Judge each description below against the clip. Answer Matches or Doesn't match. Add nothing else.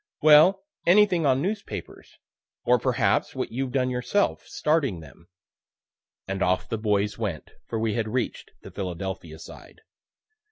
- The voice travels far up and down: Matches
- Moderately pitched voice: Doesn't match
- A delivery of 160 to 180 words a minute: Doesn't match